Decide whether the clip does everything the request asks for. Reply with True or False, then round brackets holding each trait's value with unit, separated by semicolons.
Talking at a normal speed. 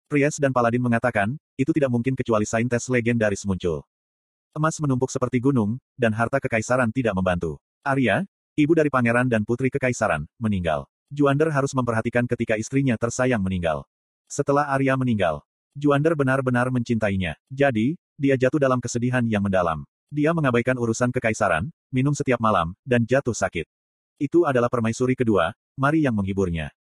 False (145 wpm)